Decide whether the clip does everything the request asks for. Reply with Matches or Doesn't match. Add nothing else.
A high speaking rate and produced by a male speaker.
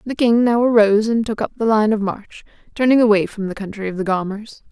Doesn't match